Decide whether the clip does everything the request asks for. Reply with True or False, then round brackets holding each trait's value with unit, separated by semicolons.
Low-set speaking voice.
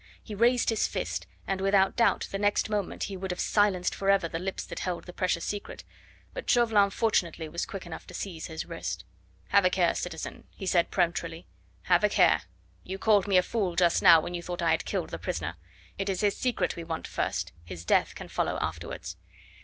False (185 Hz)